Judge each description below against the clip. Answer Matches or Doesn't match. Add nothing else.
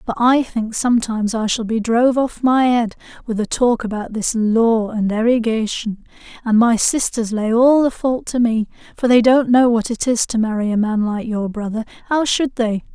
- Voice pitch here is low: Doesn't match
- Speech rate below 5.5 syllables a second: Matches